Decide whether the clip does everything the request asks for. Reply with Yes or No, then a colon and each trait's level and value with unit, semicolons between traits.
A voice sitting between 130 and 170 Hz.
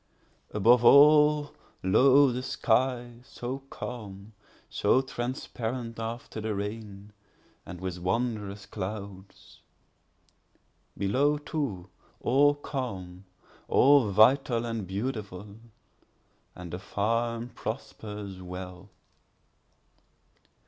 No: low, 115 Hz